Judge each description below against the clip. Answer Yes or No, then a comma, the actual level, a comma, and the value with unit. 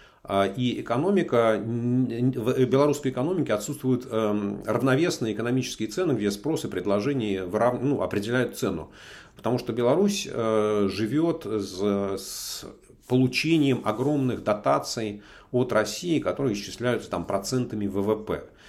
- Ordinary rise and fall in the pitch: Yes, average, 3.8 semitones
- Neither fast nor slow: No, slow, 105 wpm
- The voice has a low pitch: Yes, low, 120 Hz